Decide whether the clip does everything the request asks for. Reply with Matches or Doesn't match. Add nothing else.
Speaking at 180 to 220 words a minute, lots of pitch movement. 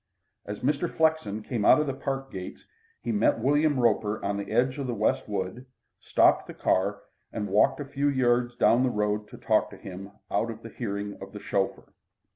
Doesn't match